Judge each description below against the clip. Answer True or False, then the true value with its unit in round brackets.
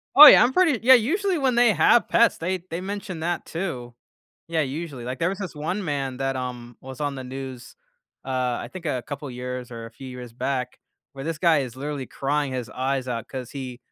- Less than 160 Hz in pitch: True (140 Hz)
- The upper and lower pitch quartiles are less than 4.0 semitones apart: False (5.5 semitones)